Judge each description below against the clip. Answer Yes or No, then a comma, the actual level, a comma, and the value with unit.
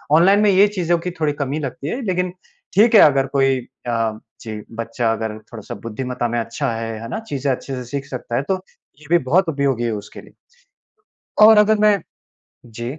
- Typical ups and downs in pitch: No, wide, 7.5 semitones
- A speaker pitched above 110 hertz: Yes, low, 135 Hz